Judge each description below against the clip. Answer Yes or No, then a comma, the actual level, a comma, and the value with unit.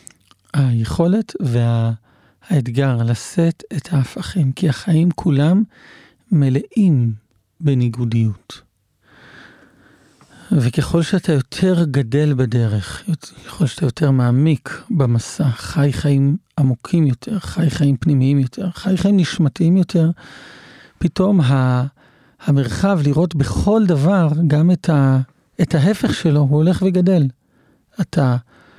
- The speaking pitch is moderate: Yes, medium, 145 Hz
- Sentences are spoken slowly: Yes, slow, 95 wpm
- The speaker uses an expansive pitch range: No, average, 4.9 semitones